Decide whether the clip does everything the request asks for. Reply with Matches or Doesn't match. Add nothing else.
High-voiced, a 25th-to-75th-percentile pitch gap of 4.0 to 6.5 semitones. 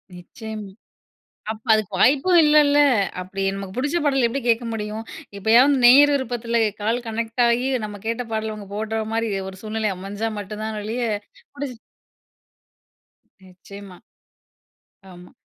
Doesn't match